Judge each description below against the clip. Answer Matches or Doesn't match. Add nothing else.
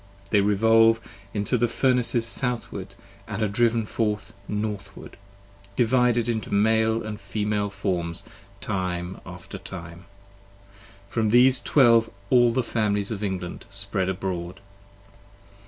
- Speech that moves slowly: Matches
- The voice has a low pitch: Matches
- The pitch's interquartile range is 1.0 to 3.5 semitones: Matches